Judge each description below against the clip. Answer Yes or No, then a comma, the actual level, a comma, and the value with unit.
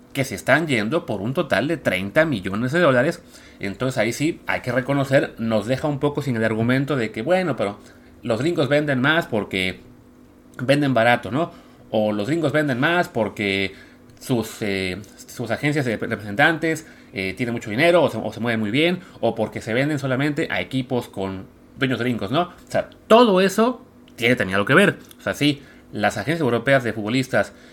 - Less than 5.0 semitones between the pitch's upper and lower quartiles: No, wide, 5.6 semitones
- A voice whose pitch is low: Yes, low, 125 Hz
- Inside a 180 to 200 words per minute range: Yes, fast, 190 wpm